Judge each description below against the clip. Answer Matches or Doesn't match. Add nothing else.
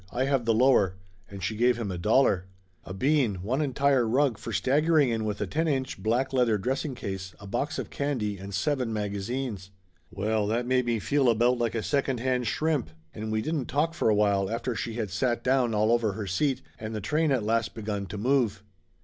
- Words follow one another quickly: Matches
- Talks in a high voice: Doesn't match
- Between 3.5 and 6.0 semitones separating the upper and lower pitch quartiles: Matches